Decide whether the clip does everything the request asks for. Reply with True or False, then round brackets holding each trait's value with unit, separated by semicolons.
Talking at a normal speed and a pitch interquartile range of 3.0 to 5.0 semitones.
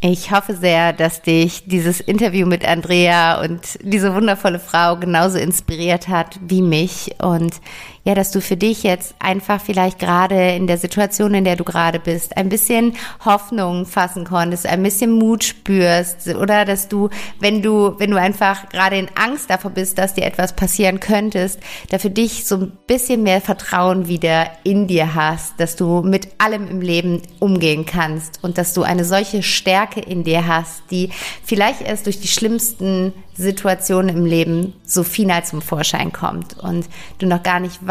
False (175 wpm; 2.4 semitones)